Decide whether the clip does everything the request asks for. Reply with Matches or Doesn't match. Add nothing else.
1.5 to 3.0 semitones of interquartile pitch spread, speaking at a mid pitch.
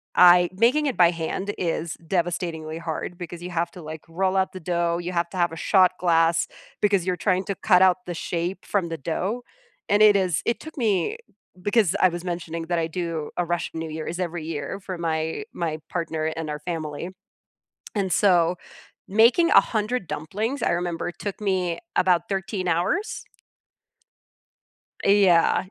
Matches